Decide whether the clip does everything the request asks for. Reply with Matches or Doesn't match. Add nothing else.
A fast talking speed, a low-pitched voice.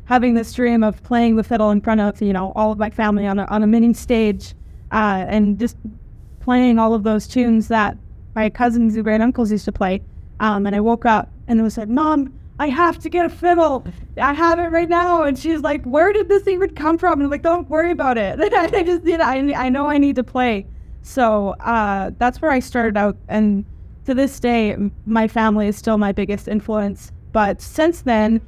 Doesn't match